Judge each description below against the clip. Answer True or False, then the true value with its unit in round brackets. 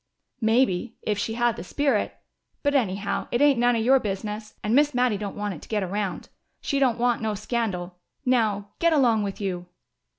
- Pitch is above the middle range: True (220 Hz)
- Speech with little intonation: False (3.5 semitones)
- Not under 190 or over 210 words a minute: True (195 wpm)